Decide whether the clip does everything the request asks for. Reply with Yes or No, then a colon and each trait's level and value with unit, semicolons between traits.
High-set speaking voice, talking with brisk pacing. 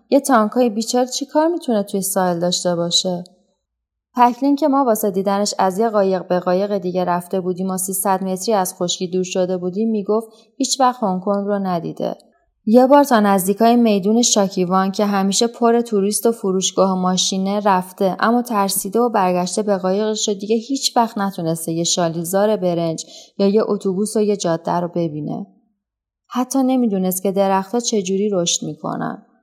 Yes: high, 200 Hz; fast, 165 wpm